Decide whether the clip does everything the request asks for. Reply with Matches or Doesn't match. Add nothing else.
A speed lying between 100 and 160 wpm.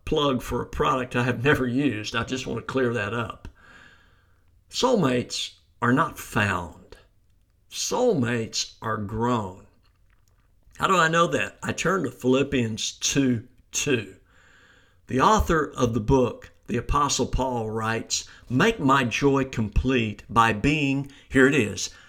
Matches